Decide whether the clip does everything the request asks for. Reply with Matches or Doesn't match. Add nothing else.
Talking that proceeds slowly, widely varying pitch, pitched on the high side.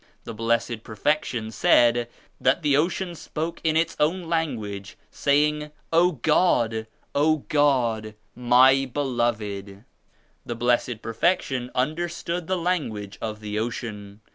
Doesn't match